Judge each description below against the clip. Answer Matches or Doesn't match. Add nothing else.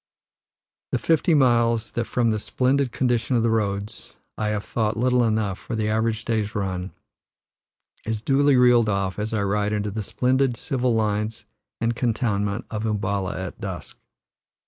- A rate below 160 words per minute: Doesn't match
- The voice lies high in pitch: Doesn't match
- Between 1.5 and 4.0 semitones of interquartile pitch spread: Matches